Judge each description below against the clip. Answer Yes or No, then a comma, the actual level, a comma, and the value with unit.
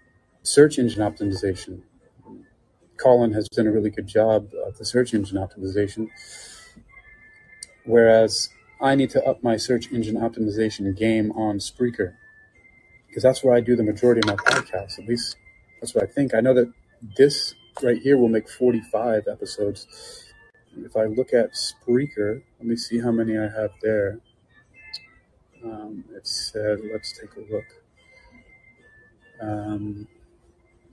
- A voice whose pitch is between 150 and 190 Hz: No, low, 110 Hz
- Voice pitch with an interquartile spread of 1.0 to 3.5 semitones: Yes, narrow, 2.4 semitones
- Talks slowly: No, average, 145 wpm